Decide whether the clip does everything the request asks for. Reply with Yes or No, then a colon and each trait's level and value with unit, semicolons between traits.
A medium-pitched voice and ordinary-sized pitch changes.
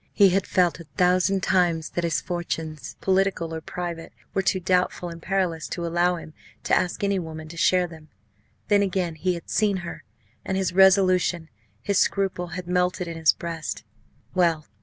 No: medium, 180 Hz; narrow, 2.1 semitones